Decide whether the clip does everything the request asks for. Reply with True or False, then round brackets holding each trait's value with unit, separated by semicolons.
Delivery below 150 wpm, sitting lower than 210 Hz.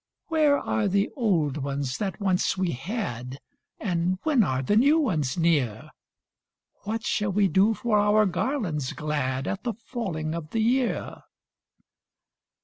True (140 wpm; 190 Hz)